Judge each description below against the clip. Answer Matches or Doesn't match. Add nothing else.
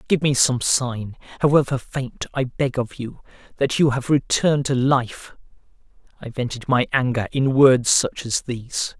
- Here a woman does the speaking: Doesn't match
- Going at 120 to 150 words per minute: Doesn't match